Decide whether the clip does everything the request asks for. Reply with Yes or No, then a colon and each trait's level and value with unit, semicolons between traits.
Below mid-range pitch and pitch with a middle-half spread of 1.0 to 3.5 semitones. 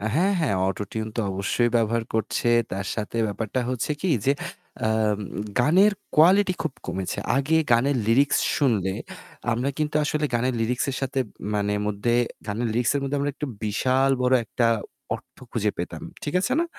No: low, 125 Hz; average, 4.7 semitones